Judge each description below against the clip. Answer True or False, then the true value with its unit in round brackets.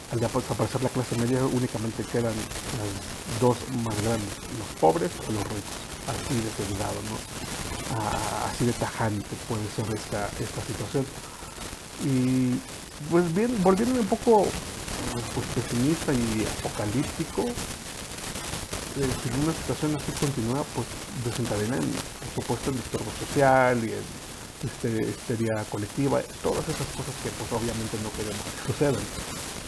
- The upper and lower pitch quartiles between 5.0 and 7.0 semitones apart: False (3.4 semitones)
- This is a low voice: True (120 Hz)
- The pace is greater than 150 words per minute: False (135 wpm)